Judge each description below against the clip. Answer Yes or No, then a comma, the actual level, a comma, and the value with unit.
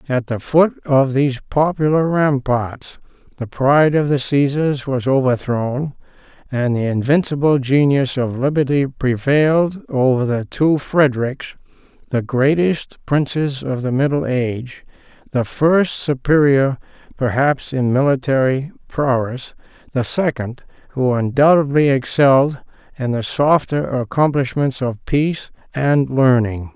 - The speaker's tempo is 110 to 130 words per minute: Yes, slow, 115 wpm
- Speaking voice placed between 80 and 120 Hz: No, low, 135 Hz